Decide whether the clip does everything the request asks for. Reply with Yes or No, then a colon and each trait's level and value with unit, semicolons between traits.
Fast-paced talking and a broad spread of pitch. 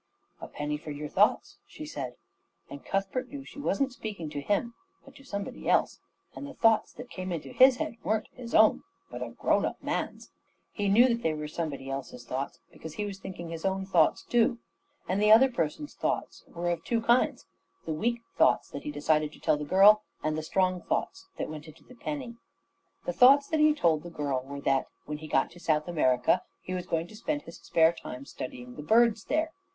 Yes: fast, 215 wpm; wide, 7.5 semitones